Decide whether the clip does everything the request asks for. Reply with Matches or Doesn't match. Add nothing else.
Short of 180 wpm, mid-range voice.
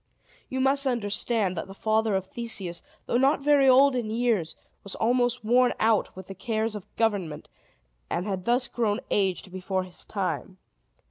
Doesn't match